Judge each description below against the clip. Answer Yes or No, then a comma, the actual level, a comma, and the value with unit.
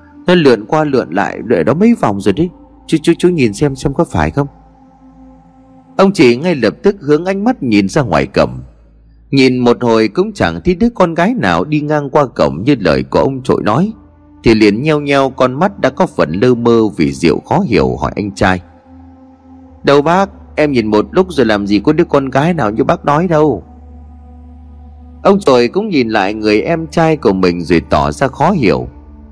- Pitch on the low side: Yes, low, 130 Hz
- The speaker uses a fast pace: No, average, 210 wpm